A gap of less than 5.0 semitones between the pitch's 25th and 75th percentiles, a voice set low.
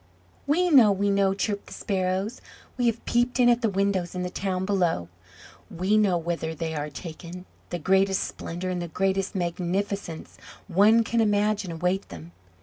No: average, 2.9 semitones; high, 190 Hz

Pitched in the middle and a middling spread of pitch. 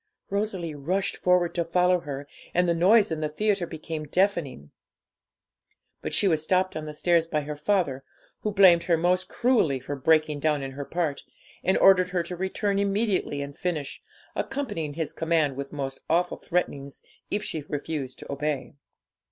Yes: medium, 165 Hz; average, 3.9 semitones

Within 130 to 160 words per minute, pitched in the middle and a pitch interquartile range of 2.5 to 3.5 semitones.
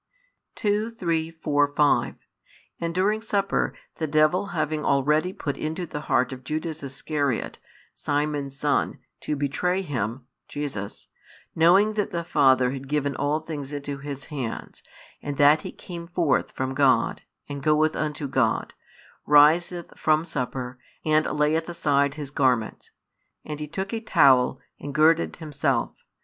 Yes: average, 140 wpm; medium, 150 Hz; average, 2.9 semitones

